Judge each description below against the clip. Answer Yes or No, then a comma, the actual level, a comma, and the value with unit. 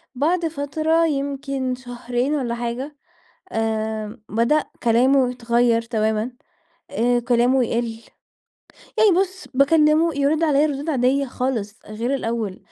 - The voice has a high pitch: Yes, very high, 255 Hz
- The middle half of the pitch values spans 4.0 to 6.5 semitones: No, average, 3.5 semitones